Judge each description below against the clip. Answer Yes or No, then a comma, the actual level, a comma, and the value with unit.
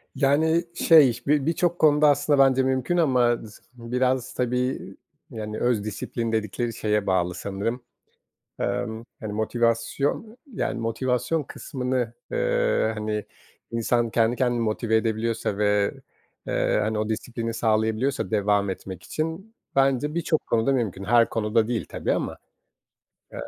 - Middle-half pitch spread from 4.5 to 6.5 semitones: No, average, 3.8 semitones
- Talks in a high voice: No, low, 120 Hz